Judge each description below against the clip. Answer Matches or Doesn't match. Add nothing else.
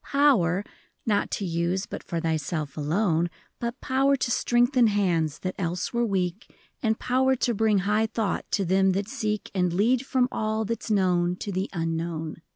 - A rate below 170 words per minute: Doesn't match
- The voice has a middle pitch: Doesn't match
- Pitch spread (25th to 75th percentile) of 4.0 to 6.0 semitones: Matches